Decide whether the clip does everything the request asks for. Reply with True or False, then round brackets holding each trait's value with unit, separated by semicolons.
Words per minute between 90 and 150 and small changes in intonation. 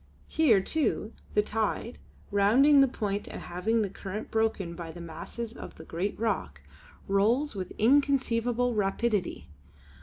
False (140 wpm; 3.5 semitones)